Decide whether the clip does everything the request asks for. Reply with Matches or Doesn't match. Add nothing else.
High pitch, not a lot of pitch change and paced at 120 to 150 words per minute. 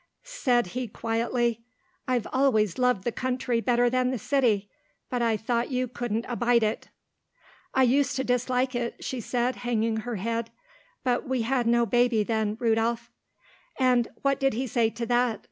Doesn't match